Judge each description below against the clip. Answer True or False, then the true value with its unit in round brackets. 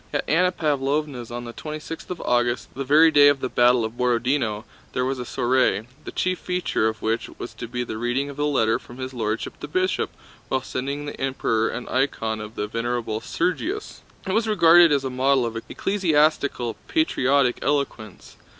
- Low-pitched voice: True (130 Hz)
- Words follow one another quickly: False (190 wpm)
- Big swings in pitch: False (3.9 semitones)